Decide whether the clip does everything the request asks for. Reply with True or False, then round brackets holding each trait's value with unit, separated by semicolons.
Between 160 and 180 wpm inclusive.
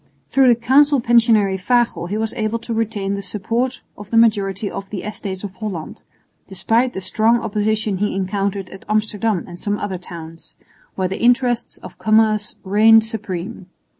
True (165 wpm)